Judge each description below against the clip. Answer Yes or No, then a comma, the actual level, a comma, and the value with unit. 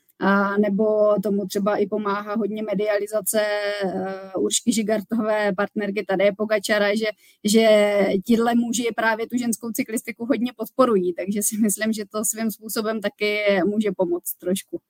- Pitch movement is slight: Yes, narrow, 1.5 semitones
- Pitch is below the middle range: No, high, 210 Hz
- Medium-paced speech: Yes, average, 140 wpm